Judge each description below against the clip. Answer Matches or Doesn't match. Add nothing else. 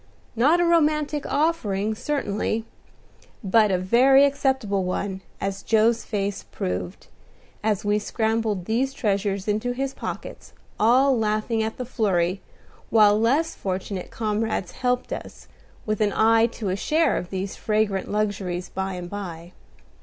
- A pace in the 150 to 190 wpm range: Doesn't match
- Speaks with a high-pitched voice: Matches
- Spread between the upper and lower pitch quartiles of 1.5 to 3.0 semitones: Doesn't match